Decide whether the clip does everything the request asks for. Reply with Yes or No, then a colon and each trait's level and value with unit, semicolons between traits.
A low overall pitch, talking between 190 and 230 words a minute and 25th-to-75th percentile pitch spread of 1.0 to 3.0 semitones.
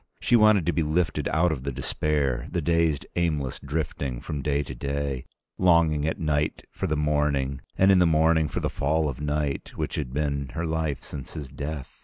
Yes: very low, 75 Hz; average, 200 wpm; narrow, 2.5 semitones